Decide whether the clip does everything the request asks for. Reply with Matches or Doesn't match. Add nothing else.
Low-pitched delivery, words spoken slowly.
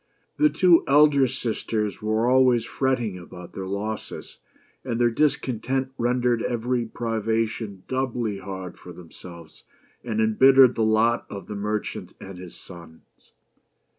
Matches